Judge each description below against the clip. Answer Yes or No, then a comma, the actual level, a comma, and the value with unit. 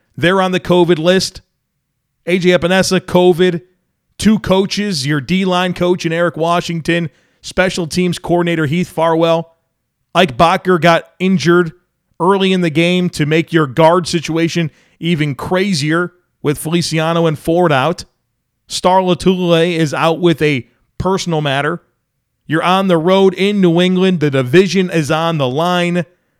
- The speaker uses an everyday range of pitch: No, narrow, 2.1 semitones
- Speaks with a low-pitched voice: No, medium, 170 Hz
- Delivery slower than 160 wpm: Yes, average, 145 wpm